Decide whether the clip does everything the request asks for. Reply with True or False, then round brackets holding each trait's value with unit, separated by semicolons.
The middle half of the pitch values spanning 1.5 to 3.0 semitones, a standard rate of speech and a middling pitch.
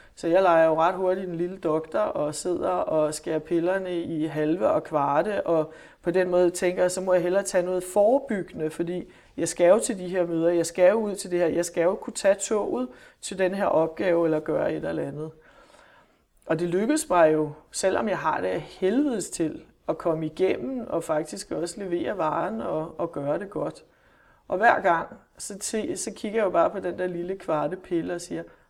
True (2.6 semitones; 215 wpm; 180 Hz)